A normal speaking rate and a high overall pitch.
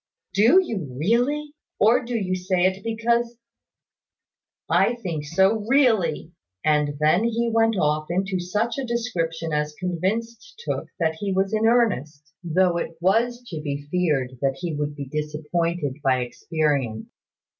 No: average, 150 wpm; medium, 180 Hz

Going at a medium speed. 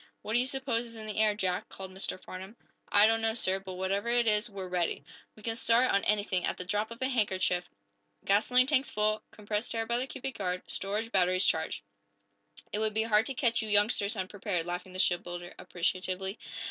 No: fast, 210 wpm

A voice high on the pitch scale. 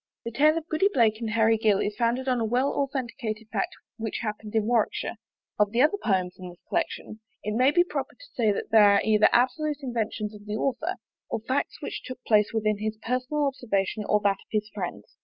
Yes: high, 225 Hz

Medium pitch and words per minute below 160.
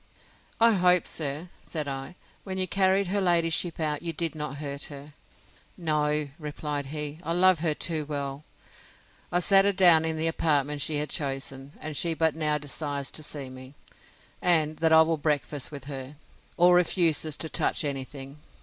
No: medium, 155 Hz; average, 175 wpm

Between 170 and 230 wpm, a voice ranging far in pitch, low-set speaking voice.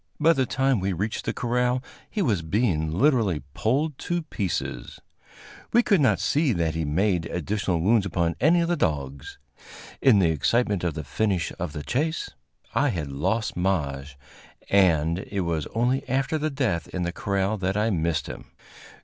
Yes: average, 175 wpm; wide, 7.4 semitones; low, 100 Hz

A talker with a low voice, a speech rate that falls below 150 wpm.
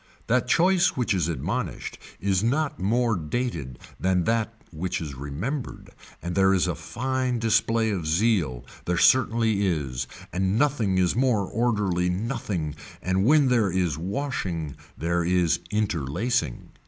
Yes: very low, 95 Hz; average, 140 wpm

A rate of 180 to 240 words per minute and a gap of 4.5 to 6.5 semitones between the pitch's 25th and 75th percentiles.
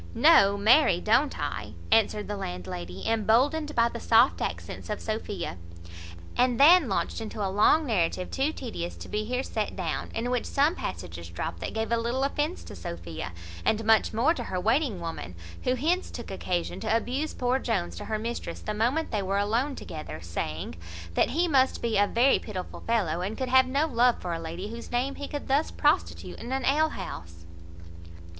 Yes: average, 190 wpm; wide, 5.6 semitones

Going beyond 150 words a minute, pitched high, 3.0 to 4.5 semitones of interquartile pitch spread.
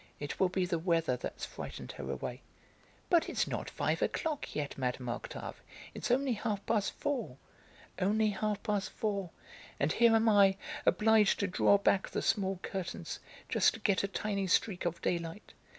Yes: average, 170 wpm; high, 200 Hz; average, 3.7 semitones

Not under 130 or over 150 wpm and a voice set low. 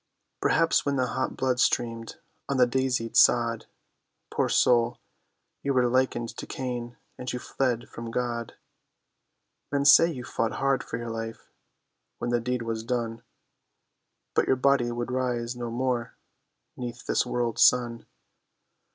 Yes: average, 145 wpm; low, 120 Hz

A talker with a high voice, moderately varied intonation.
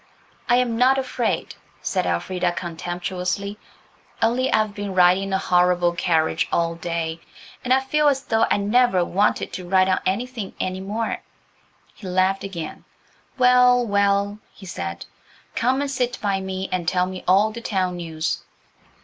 Yes: high, 195 Hz; average, 4.4 semitones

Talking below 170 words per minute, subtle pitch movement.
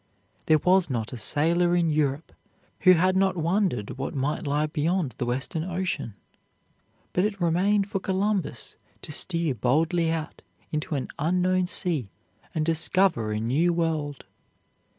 No: average, 145 wpm; average, 4.0 semitones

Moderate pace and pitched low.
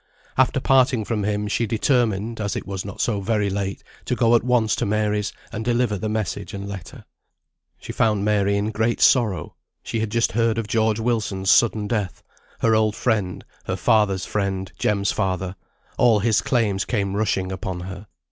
Yes: average, 180 wpm; low, 105 Hz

